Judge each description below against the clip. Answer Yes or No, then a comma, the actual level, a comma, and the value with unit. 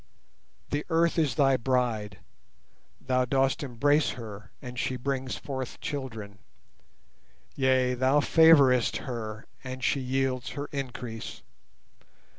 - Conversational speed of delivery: No, slow, 110 wpm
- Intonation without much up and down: Yes, narrow, 2.3 semitones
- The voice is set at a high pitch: No, low, 130 Hz